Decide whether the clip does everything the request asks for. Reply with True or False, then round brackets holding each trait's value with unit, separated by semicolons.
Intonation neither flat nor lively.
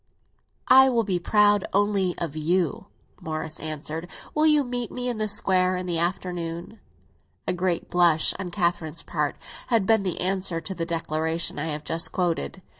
True (3.7 semitones)